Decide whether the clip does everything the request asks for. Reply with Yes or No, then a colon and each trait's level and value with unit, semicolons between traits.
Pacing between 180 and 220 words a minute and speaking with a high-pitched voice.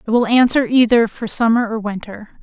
Yes: average, 200 wpm; high, 225 Hz